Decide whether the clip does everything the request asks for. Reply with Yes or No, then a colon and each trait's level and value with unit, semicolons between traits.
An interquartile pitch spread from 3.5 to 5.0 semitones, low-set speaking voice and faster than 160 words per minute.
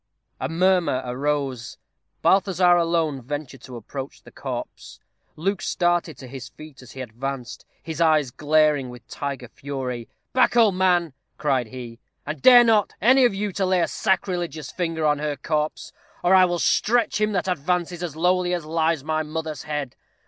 No: average, 4.7 semitones; medium, 155 Hz; average, 170 wpm